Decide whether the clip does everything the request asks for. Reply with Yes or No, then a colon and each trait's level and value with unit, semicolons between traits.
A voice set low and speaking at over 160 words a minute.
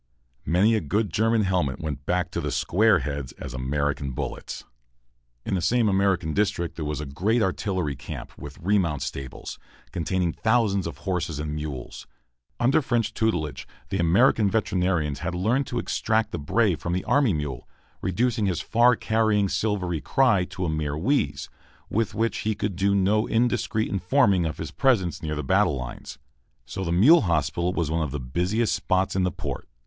Yes: very low, 90 Hz; average, 175 wpm